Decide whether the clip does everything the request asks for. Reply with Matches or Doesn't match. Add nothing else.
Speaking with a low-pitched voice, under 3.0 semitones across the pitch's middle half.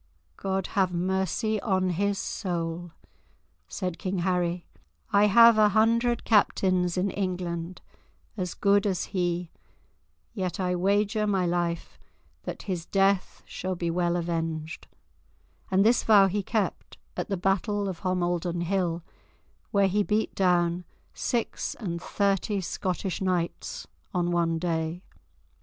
Doesn't match